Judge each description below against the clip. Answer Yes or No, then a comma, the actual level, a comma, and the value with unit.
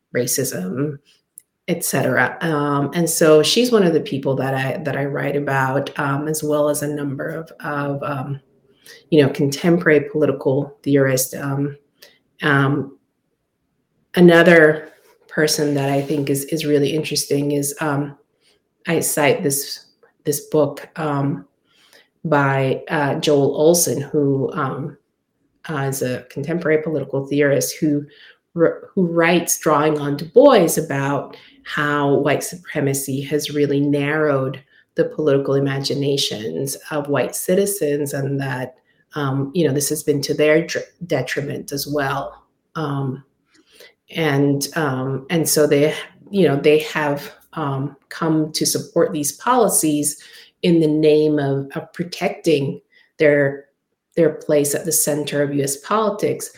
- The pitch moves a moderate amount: No, narrow, 1.9 semitones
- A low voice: No, medium, 145 Hz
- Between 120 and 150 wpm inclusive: Yes, slow, 135 wpm